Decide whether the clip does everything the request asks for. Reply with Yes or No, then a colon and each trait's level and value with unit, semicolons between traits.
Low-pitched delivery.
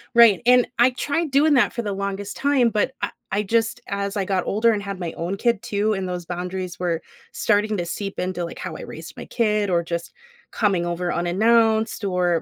No: high, 200 Hz